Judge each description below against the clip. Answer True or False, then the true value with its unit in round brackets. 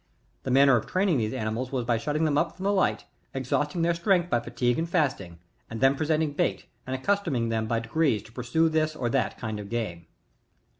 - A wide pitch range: True (5.7 semitones)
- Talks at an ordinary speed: False (215 wpm)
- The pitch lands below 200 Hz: True (135 Hz)